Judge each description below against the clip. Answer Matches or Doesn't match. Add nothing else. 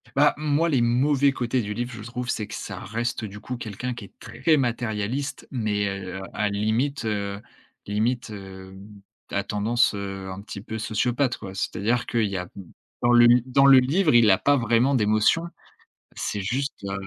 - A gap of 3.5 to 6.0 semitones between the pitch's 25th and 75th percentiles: Matches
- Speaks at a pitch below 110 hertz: Doesn't match